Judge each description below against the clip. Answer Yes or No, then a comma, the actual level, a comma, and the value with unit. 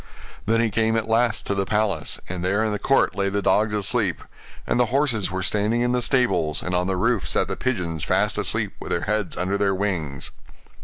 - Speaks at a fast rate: Yes, fast, 220 wpm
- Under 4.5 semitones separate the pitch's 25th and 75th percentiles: Yes, average, 3.4 semitones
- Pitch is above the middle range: No, low, 105 Hz